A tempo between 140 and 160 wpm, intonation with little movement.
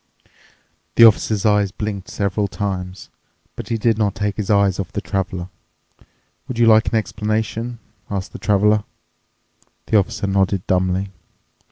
Yes: average, 145 wpm; narrow, 1.9 semitones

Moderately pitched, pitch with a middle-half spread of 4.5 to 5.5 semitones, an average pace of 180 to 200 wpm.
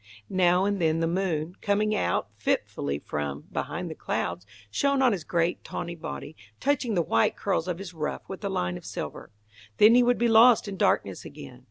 Yes: medium, 180 Hz; average, 5.1 semitones; average, 195 wpm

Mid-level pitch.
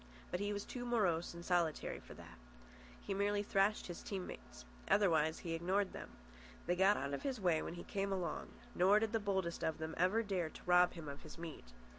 Yes: medium, 180 Hz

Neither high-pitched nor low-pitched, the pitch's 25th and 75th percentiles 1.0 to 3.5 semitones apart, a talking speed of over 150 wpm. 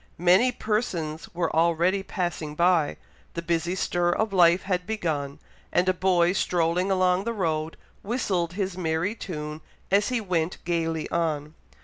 No: medium, 175 Hz; narrow, 2.6 semitones; average, 145 wpm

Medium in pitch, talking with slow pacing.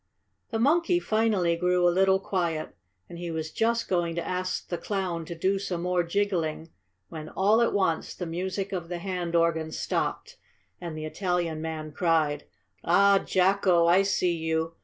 No: medium, 175 Hz; average, 170 wpm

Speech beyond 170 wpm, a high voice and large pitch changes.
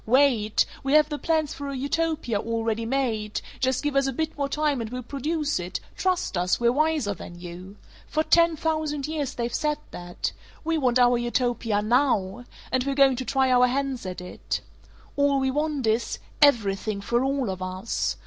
No: average, 185 wpm; very high, 260 Hz; average, 4.5 semitones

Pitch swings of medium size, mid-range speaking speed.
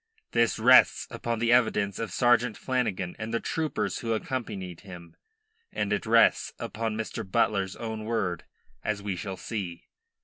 Yes: average, 3.4 semitones; average, 150 wpm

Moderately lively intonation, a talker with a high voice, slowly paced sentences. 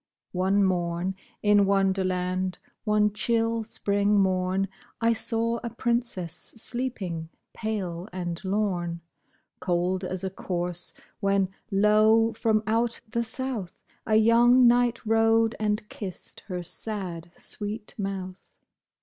Yes: average, 3.4 semitones; high, 200 Hz; slow, 120 wpm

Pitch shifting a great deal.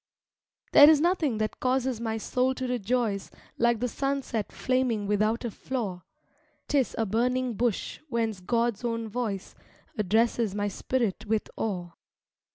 No: average, 3.0 semitones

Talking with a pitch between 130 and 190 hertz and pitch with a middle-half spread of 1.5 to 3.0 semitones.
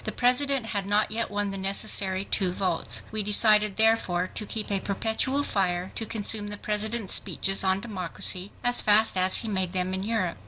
No: high, 205 Hz; narrow, 2.6 semitones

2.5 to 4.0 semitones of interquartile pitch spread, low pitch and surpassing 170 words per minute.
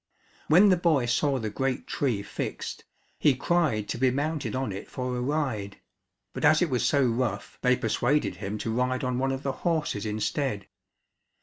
No: average, 4.5 semitones; low, 130 Hz; average, 185 wpm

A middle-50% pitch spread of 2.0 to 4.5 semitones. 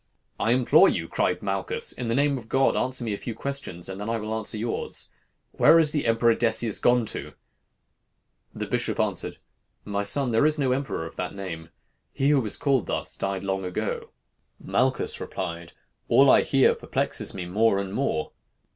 No: average, 5.2 semitones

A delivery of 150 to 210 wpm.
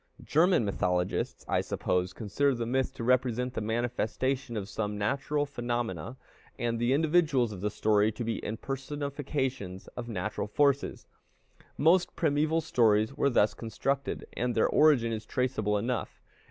No: average, 140 wpm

